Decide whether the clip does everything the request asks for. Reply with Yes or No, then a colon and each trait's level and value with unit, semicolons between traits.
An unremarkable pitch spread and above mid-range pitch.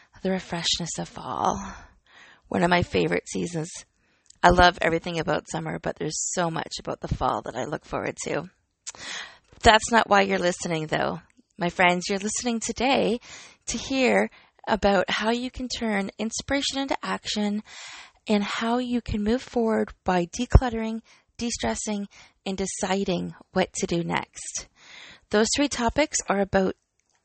Yes: average, 4.2 semitones; high, 210 Hz